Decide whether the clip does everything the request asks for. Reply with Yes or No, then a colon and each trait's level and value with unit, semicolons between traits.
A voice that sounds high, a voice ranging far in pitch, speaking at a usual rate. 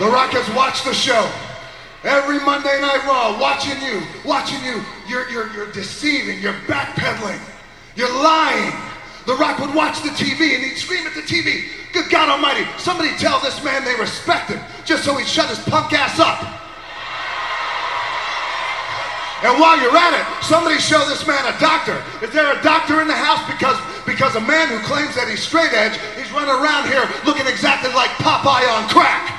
No: very high, 280 Hz; average, 3.4 semitones; average, 185 wpm